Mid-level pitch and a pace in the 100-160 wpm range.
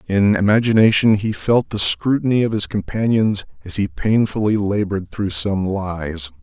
No: low, 100 Hz; average, 150 wpm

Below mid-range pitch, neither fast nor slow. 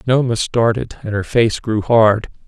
Yes: low, 115 Hz; average, 170 wpm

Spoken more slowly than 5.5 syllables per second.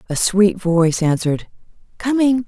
Yes: 5.0 syllables/s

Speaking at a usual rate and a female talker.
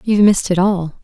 No: fast, 235 wpm; female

